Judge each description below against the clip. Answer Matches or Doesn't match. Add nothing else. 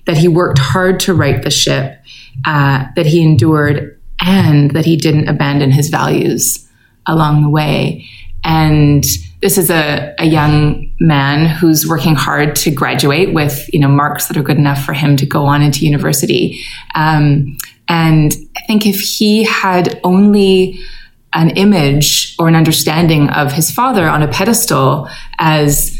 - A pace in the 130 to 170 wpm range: Matches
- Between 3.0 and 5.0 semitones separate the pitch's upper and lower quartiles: Doesn't match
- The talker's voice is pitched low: Doesn't match